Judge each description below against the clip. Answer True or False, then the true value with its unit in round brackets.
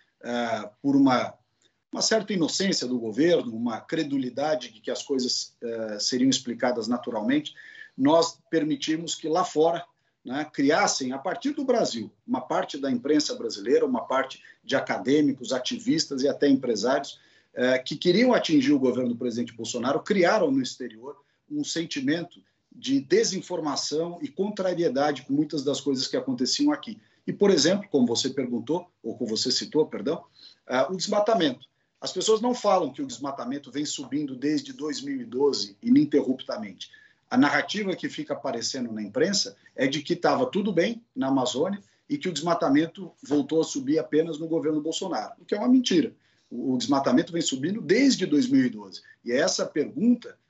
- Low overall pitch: False (165 Hz)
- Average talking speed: True (160 wpm)